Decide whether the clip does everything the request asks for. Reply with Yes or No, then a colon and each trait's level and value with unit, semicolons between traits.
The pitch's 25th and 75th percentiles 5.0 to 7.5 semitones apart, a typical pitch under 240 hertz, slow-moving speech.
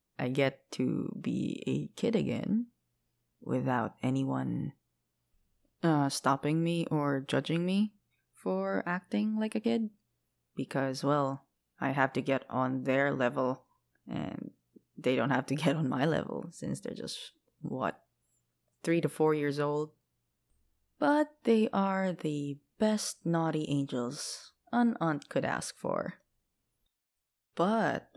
Yes: wide, 5.5 semitones; medium, 140 Hz; slow, 130 wpm